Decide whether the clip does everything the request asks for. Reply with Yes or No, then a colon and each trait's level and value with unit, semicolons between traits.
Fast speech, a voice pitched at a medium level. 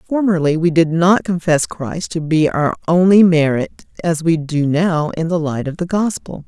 No: average, 195 wpm; medium, 165 Hz